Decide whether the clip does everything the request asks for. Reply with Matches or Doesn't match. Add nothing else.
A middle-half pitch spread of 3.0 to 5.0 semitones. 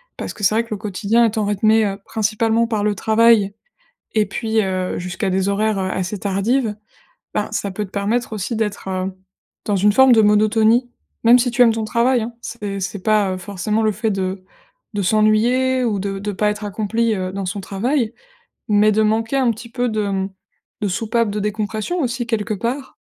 Doesn't match